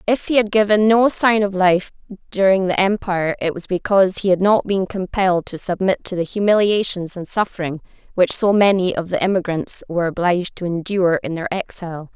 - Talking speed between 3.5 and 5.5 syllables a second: No, 5.7 syllables/s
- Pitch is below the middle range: No, high, 190 Hz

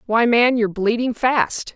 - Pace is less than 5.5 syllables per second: Yes, 4.4 syllables/s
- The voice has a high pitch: Yes, high, 230 Hz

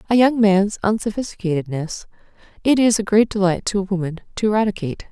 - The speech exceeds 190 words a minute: No, average, 165 wpm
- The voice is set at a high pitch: Yes, high, 200 Hz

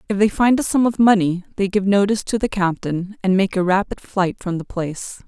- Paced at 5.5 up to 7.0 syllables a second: Yes, 5.6 syllables/s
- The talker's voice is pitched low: No, high, 195 Hz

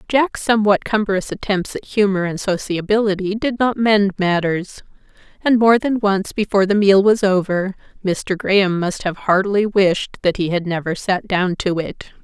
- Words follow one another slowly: No, average, 170 wpm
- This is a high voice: Yes, high, 195 Hz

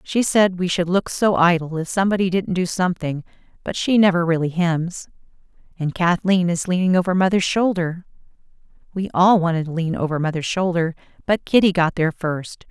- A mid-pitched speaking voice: Yes, medium, 175 Hz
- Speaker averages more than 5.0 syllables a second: Yes, 5.4 syllables/s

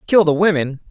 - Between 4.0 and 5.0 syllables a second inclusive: No, 5.7 syllables/s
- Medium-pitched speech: Yes, medium, 165 Hz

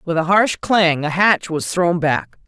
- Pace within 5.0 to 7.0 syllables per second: No, 3.9 syllables/s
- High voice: No, medium, 170 Hz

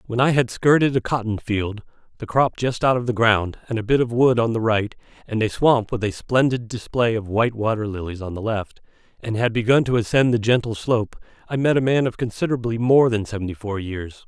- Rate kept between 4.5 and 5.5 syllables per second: No, 5.7 syllables/s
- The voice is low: Yes, low, 115 Hz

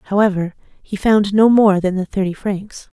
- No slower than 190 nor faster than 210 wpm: No, average, 180 wpm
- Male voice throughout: No, female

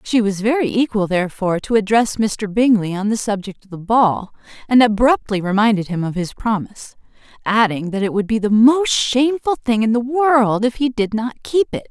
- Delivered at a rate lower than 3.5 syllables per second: No, 5.3 syllables/s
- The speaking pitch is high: Yes, high, 220 Hz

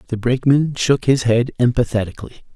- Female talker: No, male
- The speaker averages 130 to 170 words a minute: Yes, average, 140 wpm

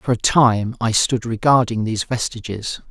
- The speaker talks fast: No, average, 165 wpm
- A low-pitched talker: Yes, low, 115 Hz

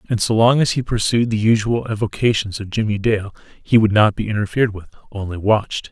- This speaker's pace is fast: No, average, 195 wpm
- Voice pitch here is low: Yes, low, 110 Hz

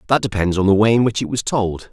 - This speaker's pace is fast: Yes, fast, 315 wpm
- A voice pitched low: Yes, low, 105 Hz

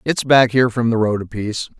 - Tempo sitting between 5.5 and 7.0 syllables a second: Yes, 6.2 syllables/s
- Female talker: No, male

